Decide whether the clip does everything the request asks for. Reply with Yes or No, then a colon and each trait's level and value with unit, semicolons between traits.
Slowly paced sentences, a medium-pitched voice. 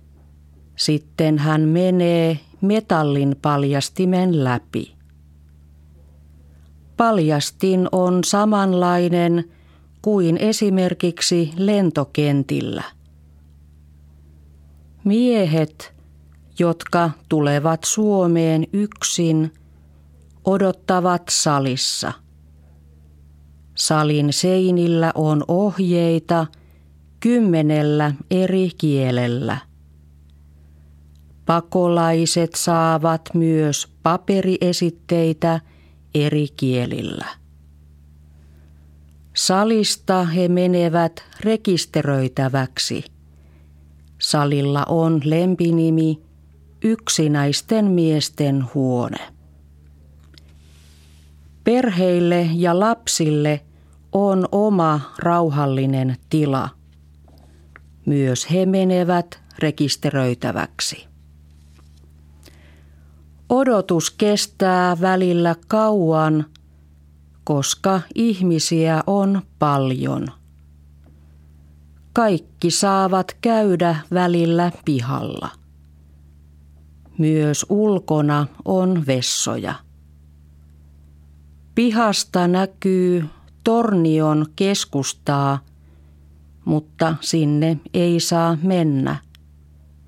Yes: slow, 55 wpm; medium, 150 Hz